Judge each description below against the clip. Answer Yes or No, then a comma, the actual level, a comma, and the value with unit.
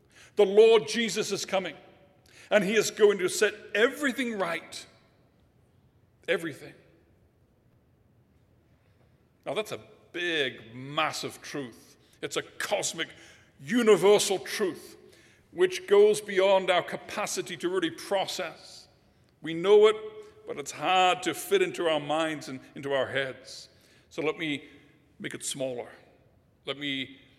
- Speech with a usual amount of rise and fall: No, wide, 8.5 semitones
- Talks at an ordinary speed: No, slow, 125 wpm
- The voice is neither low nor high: Yes, medium, 180 Hz